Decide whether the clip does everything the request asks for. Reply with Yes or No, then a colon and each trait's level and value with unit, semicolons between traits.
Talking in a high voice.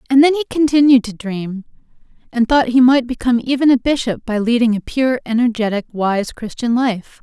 Yes: high, 240 Hz